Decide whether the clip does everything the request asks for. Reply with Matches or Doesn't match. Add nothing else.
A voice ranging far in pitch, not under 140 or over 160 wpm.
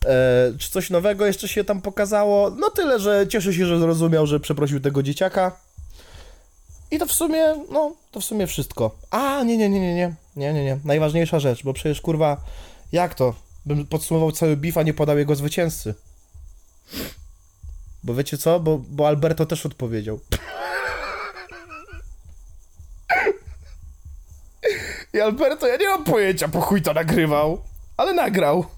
Matches